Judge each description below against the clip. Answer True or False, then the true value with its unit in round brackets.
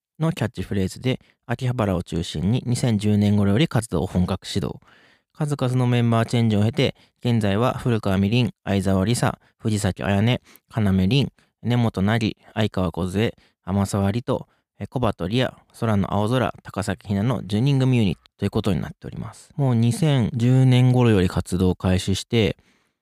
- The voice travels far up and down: False (4.0 semitones)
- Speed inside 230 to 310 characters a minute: True (305 characters per minute)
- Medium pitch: False (110 Hz)